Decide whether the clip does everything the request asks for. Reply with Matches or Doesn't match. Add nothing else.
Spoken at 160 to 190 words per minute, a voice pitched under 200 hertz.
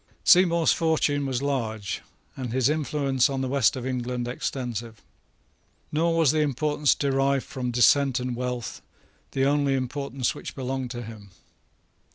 Doesn't match